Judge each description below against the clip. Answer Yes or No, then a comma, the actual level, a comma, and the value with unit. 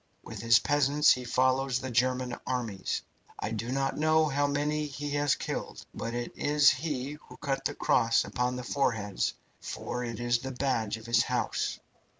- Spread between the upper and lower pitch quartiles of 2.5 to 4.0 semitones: Yes, average, 3.4 semitones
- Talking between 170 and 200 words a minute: Yes, average, 175 wpm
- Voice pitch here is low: Yes, low, 130 Hz